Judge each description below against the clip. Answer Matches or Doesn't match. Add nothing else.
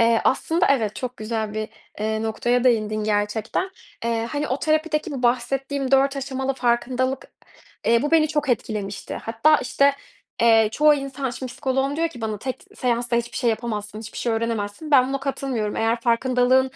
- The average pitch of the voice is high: Matches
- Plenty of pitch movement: Doesn't match